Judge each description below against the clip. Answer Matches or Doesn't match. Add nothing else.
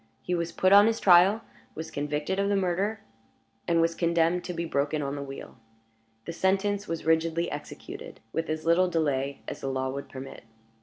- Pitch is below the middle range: Doesn't match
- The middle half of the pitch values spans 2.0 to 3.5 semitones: Doesn't match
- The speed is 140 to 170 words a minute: Doesn't match